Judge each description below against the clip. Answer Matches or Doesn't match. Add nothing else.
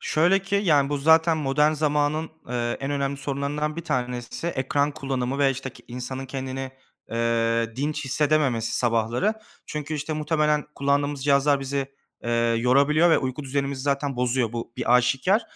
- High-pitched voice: Doesn't match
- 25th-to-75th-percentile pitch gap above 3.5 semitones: Doesn't match